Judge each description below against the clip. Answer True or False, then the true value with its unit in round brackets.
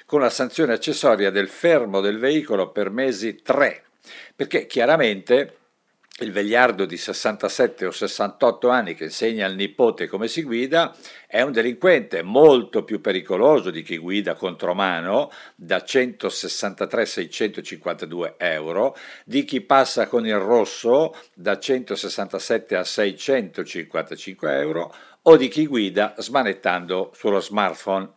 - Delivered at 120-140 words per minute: True (130 wpm)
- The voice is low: True (120 Hz)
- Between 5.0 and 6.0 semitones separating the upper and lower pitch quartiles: True (5.3 semitones)